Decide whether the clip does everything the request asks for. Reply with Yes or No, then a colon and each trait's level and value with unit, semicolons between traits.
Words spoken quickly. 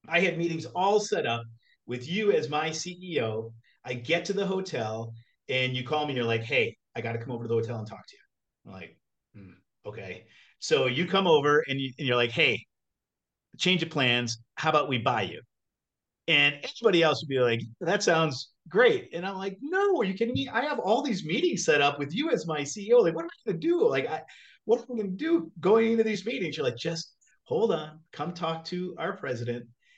Yes: fast, 230 wpm